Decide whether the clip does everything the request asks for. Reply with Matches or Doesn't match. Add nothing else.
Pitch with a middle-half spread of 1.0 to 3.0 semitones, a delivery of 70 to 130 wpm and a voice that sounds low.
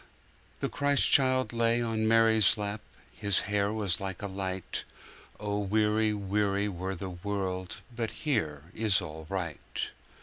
Matches